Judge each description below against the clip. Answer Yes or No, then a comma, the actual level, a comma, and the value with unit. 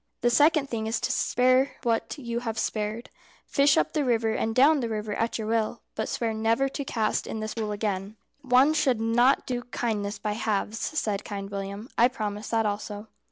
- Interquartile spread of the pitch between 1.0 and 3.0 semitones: Yes, average, 2.7 semitones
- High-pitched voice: Yes, high, 225 Hz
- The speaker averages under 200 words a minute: No, fast, 205 wpm